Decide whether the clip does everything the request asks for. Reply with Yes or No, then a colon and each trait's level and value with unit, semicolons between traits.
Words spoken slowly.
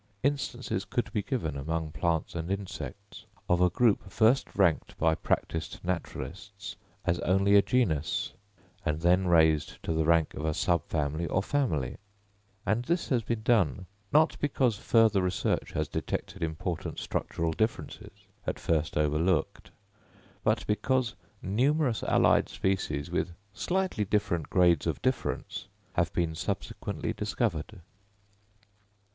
Yes: slow, 130 wpm